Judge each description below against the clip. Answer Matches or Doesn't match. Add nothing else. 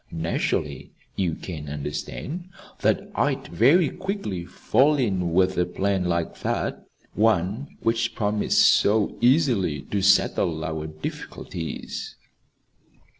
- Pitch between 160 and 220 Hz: Doesn't match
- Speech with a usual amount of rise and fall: Doesn't match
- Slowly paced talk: Matches